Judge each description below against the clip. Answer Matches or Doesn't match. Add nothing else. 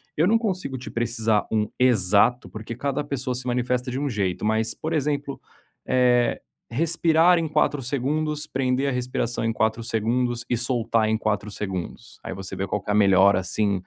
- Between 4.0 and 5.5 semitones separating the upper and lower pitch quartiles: Matches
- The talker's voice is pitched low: Matches